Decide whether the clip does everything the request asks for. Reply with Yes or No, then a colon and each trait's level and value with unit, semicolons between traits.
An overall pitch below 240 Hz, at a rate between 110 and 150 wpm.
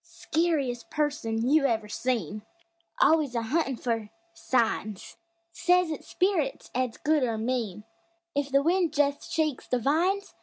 No: very high, 275 Hz; average, 140 wpm